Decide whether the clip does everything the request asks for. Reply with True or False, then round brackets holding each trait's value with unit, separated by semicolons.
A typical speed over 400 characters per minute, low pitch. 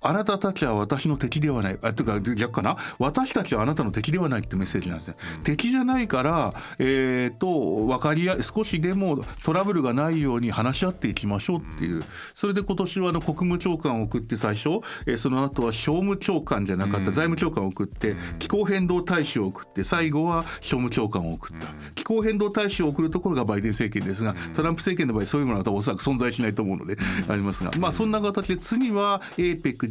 False (445 characters per minute; 145 Hz)